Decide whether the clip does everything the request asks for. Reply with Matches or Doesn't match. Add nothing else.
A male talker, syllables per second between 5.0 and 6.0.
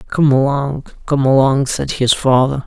Doesn't match